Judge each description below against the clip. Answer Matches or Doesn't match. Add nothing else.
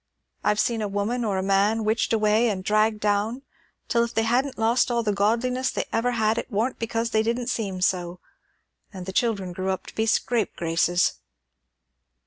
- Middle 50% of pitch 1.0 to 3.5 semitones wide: Matches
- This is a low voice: Doesn't match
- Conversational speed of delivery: Matches